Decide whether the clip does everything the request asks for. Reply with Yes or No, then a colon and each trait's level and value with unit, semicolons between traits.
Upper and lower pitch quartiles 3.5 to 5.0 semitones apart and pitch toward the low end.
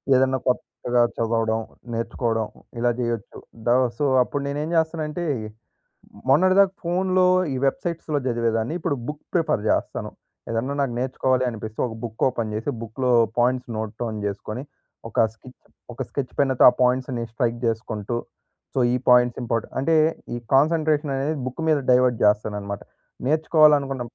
Yes: average, 4.3 semitones; low, 125 Hz